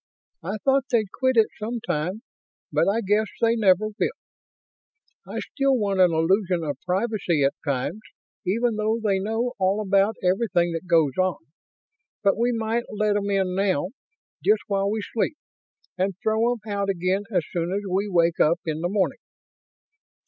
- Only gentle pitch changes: No, average, 3.4 semitones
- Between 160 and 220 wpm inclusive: Yes, average, 165 wpm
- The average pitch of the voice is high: Yes, high, 200 Hz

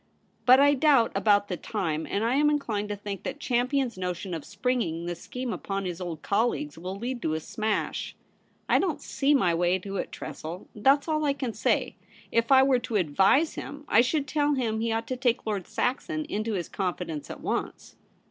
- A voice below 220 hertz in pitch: No, high, 225 Hz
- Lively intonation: Yes, wide, 6.0 semitones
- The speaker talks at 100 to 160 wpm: No, fast, 205 wpm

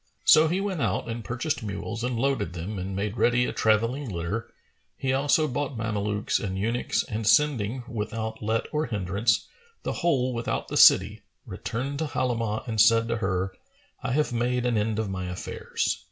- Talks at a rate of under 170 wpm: No, average, 180 wpm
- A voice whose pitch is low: Yes, low, 115 Hz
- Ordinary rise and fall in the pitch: Yes, average, 3.5 semitones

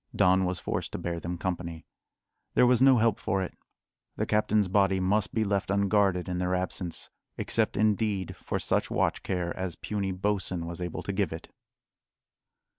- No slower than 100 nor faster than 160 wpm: No, average, 175 wpm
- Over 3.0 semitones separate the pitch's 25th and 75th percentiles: No, narrow, 2.4 semitones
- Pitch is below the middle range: Yes, very low, 95 Hz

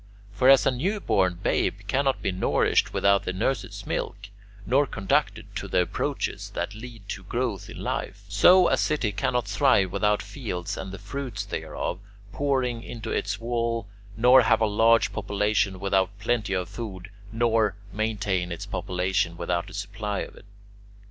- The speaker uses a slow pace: No, average, 160 wpm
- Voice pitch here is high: No, low, 105 Hz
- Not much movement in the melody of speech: No, average, 3.9 semitones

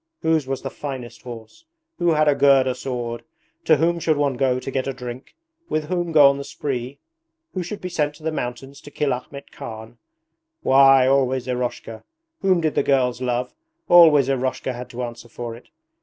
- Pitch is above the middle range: No, low, 135 Hz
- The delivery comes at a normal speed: Yes, average, 190 wpm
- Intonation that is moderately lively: Yes, average, 3.2 semitones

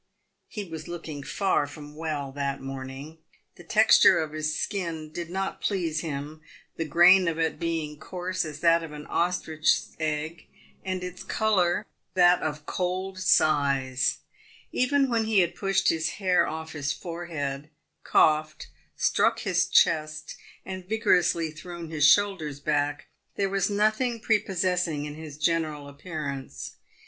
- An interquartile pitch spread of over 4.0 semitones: No, average, 3.5 semitones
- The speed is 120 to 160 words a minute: Yes, average, 145 wpm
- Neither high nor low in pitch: Yes, medium, 165 Hz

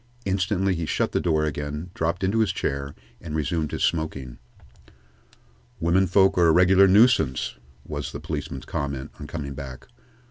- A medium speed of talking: Yes, average, 155 wpm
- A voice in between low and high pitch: No, very low, 80 Hz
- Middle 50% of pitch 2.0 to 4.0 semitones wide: No, average, 4.4 semitones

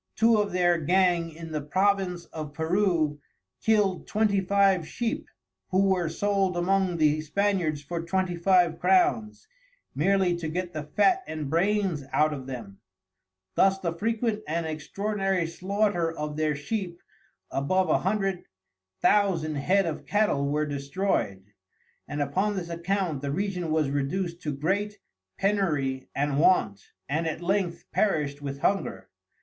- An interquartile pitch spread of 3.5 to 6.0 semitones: Yes, average, 4.4 semitones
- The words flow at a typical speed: Yes, average, 145 wpm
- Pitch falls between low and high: Yes, medium, 175 Hz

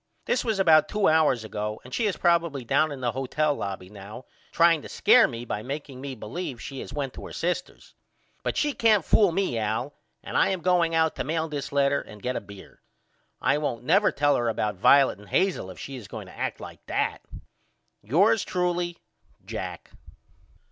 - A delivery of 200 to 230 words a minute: Yes, fast, 205 wpm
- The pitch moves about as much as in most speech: No, wide, 6.4 semitones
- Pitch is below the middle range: No, medium, 145 Hz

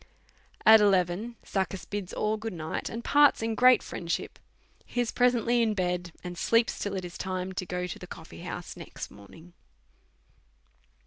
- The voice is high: Yes, high, 195 Hz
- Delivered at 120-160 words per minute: No, average, 170 wpm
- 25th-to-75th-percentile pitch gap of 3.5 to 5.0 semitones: Yes, average, 4.2 semitones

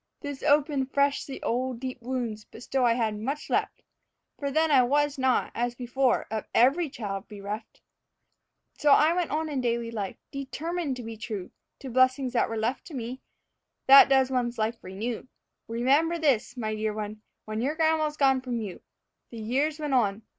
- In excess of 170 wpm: Yes, average, 180 wpm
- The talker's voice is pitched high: Yes, very high, 255 Hz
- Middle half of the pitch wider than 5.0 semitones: No, average, 3.6 semitones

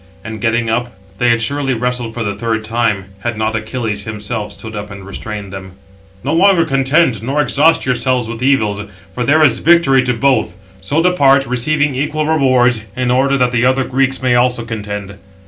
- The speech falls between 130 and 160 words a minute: No, average, 185 wpm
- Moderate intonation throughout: Yes, average, 3.6 semitones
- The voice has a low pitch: Yes, low, 125 Hz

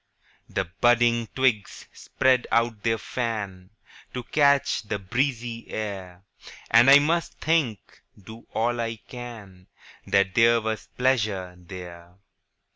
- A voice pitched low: Yes, low, 115 Hz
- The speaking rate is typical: No, slow, 120 wpm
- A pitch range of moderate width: Yes, average, 3.7 semitones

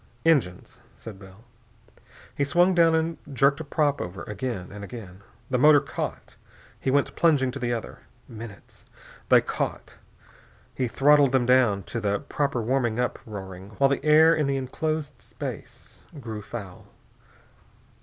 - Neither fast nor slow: Yes, average, 150 wpm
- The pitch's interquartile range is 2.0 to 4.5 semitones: No, wide, 5.5 semitones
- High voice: No, low, 130 Hz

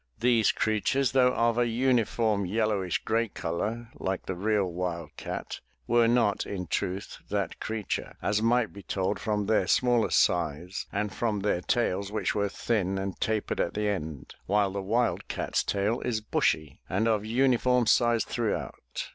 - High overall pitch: No, low, 105 Hz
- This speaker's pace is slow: No, average, 160 wpm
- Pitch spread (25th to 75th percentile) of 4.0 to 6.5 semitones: No, average, 3.3 semitones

